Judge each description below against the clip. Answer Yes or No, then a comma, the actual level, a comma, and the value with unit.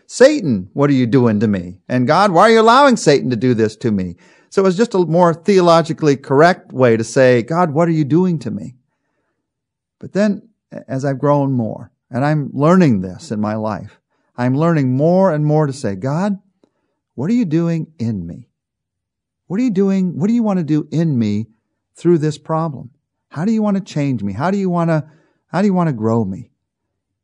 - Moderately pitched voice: Yes, medium, 150 Hz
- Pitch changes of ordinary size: No, wide, 6.8 semitones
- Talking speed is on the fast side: Yes, fast, 215 wpm